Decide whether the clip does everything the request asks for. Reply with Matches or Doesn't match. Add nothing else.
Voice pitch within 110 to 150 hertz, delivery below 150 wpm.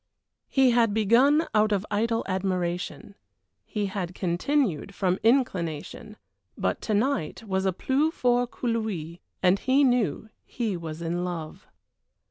Doesn't match